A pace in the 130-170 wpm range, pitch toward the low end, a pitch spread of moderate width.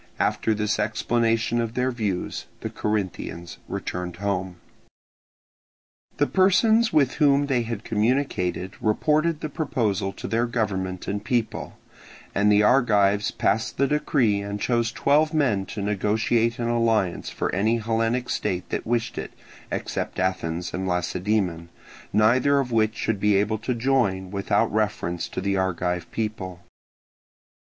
Yes: average, 140 wpm; low, 110 Hz; average, 3.7 semitones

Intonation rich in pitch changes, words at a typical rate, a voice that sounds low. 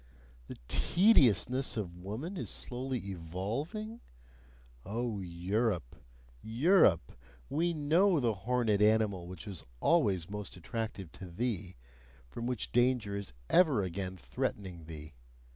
No: wide, 5.7 semitones; slow, 115 wpm; low, 105 Hz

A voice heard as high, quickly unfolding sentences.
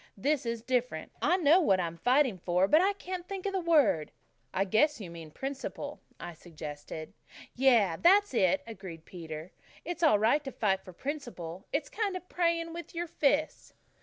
No: very high, 255 Hz; average, 180 wpm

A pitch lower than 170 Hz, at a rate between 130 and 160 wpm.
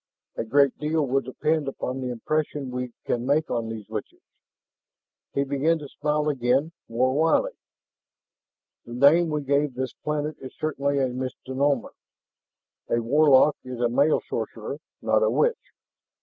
Yes: medium, 140 Hz; average, 150 wpm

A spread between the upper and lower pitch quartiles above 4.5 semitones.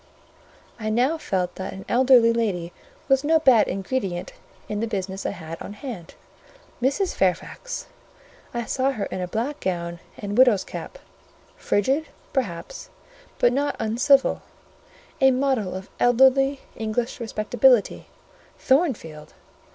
Yes: wide, 5.6 semitones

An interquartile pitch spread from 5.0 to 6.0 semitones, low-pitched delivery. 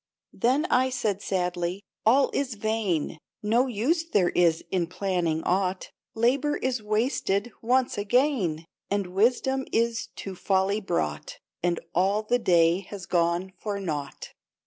No: average, 5.3 semitones; high, 200 Hz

